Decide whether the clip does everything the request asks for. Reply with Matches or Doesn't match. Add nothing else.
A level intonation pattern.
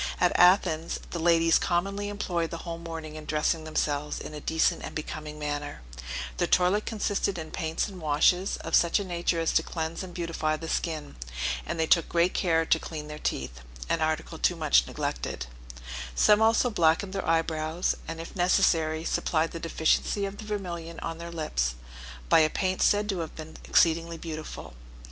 Matches